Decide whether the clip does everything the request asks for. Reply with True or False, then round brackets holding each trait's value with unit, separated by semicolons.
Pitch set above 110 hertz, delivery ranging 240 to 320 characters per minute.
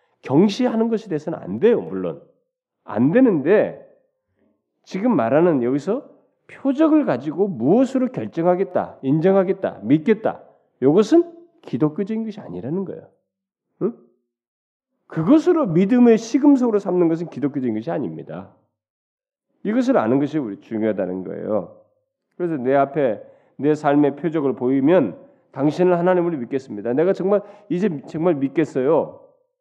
True (190 Hz; 305 characters per minute)